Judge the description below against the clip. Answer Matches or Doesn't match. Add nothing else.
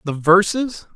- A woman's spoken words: Doesn't match